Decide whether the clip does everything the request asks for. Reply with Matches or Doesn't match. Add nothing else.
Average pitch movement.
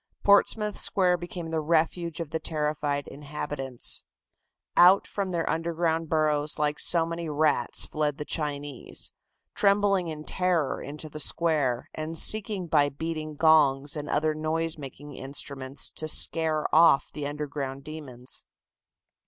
Doesn't match